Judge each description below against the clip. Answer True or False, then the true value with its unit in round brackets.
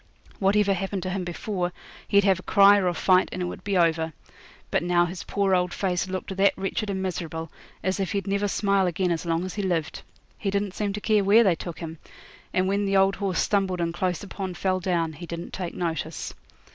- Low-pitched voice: False (185 Hz)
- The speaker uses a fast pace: True (225 wpm)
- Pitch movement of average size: False (2.3 semitones)